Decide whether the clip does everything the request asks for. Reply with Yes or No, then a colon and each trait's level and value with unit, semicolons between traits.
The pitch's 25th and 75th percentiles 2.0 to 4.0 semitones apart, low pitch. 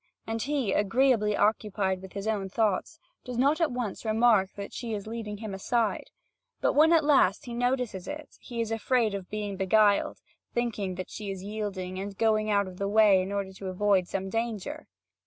No: average, 3.3 semitones; high, 210 Hz